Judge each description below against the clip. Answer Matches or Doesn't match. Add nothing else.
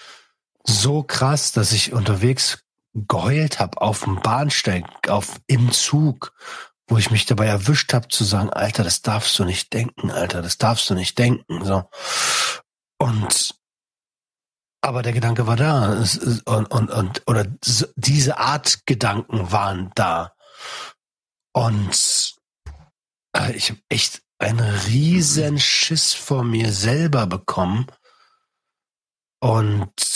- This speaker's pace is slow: Matches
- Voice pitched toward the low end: Matches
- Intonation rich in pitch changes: Doesn't match